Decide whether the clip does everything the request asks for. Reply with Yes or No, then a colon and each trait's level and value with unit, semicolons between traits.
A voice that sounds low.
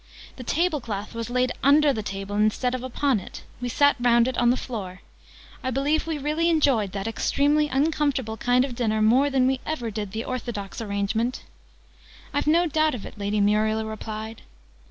No: high, 245 Hz